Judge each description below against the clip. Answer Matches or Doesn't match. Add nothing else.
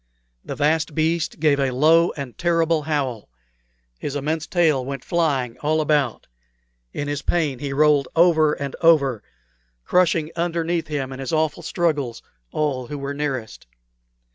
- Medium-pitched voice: Matches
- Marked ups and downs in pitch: Doesn't match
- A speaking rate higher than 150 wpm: Doesn't match